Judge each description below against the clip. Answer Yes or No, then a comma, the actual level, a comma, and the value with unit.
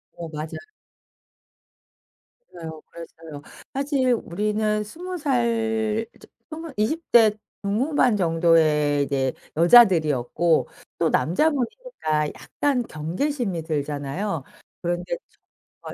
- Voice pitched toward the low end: No, high, 195 Hz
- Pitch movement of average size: No, wide, 7.4 semitones